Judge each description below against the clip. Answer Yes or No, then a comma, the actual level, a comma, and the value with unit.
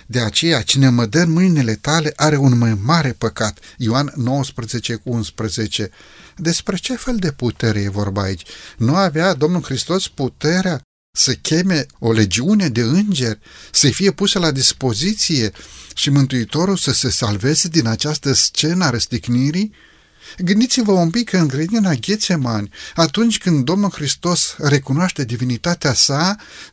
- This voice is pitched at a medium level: Yes, medium, 145 Hz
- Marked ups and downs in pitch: Yes, wide, 6.8 semitones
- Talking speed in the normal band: Yes, average, 140 wpm